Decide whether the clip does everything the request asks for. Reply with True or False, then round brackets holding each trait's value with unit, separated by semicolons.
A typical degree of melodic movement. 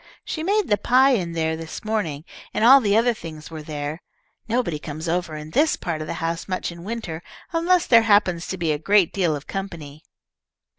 False (6.0 semitones)